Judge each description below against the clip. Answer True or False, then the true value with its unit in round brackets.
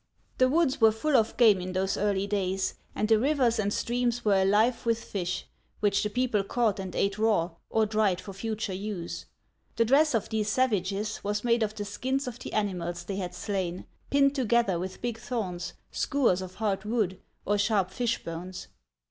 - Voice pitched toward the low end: False (210 Hz)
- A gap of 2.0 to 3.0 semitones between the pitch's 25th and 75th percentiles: False (3.6 semitones)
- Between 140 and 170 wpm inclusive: False (190 wpm)